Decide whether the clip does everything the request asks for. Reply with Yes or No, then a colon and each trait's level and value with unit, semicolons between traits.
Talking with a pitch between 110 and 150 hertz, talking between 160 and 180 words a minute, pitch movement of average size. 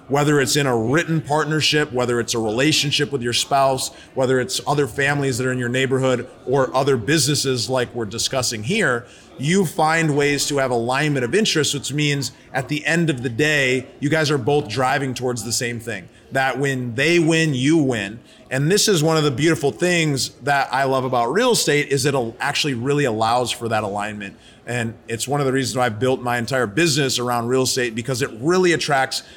No: low, 135 Hz; fast, 205 wpm; average, 3.2 semitones